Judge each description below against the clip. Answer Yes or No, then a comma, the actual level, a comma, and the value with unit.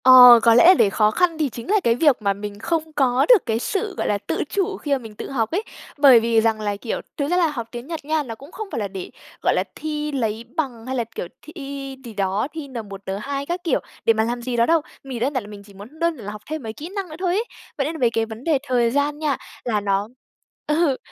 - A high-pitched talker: Yes, very high, 255 Hz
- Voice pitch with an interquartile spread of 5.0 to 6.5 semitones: Yes, wide, 5.6 semitones